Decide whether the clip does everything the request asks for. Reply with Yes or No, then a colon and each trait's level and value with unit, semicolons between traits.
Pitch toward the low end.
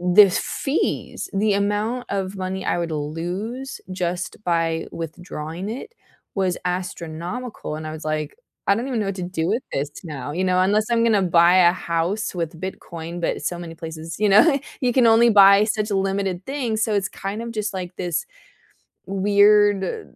No: high, 190 Hz